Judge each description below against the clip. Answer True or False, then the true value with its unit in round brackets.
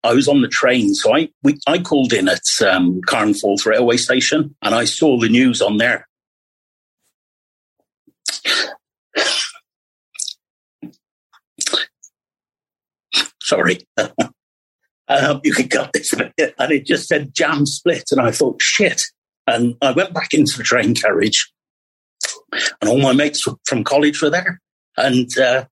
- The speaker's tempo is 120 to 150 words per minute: True (140 wpm)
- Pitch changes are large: True (6.7 semitones)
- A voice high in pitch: False (135 Hz)